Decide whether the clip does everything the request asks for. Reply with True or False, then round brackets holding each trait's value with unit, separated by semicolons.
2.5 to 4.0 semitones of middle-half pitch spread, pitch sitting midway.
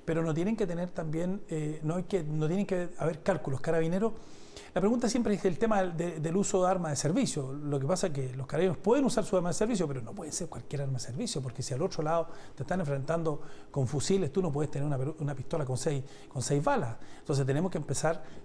False (4.6 semitones; 165 Hz)